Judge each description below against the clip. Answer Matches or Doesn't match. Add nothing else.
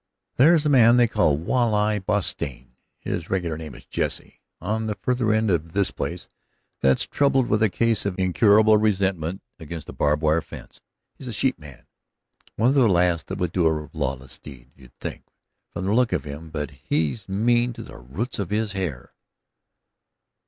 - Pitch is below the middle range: Matches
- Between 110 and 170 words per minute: Doesn't match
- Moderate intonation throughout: Doesn't match